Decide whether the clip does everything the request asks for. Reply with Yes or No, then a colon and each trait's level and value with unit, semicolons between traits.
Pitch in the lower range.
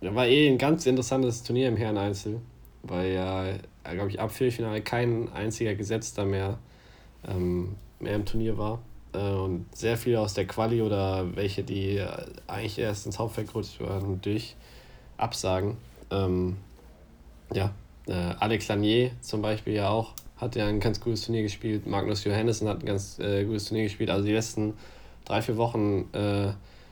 Yes: low, 105 Hz